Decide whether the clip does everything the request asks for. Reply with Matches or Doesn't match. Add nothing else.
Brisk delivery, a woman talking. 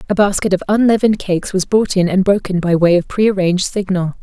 Matches